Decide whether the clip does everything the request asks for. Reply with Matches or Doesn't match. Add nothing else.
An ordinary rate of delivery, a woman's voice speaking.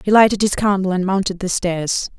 Doesn't match